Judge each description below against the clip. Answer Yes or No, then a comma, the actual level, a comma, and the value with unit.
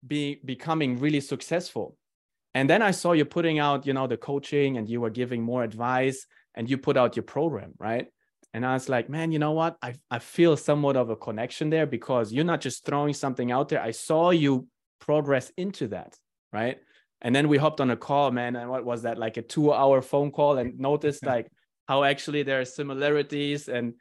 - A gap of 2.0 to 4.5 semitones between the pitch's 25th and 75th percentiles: Yes, average, 2.9 semitones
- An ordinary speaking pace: No, fast, 210 wpm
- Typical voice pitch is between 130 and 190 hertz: Yes, medium, 140 Hz